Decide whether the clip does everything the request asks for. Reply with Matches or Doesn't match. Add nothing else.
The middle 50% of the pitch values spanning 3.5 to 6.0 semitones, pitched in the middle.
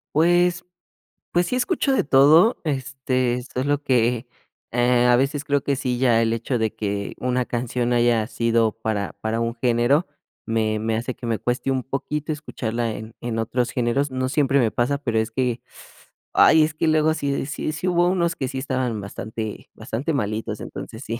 Doesn't match